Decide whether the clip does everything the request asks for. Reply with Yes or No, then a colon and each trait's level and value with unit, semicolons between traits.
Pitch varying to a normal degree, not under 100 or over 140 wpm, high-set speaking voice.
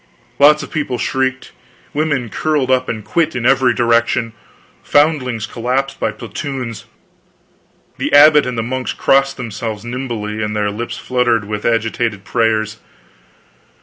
No: average, 3.2 semitones; slow, 135 wpm; low, 120 Hz